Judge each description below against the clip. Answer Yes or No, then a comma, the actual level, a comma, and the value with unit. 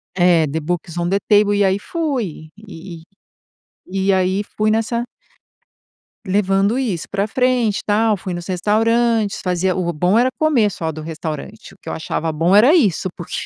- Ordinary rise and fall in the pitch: Yes, average, 4.0 semitones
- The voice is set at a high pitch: Yes, high, 195 Hz